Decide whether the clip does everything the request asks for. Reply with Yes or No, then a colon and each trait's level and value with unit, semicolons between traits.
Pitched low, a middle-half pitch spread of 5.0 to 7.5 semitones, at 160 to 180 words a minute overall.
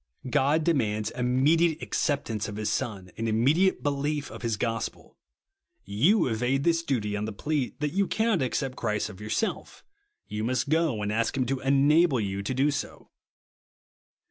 Yes: low, 130 Hz; wide, 5.5 semitones; average, 170 wpm